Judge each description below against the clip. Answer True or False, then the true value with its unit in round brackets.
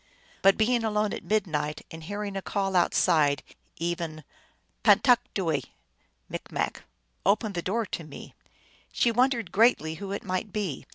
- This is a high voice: True (195 Hz)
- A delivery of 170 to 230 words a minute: False (150 wpm)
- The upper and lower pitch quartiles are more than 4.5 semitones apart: True (4.9 semitones)